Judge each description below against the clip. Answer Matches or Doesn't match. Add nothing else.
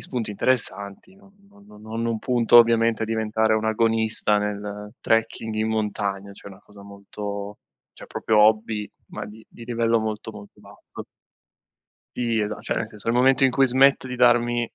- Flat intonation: Matches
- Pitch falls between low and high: Doesn't match